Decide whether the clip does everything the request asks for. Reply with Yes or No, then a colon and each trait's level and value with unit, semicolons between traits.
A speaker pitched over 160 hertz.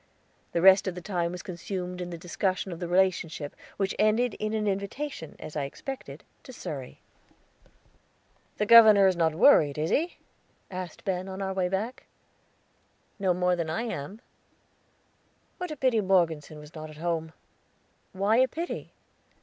Yes: medium, 185 Hz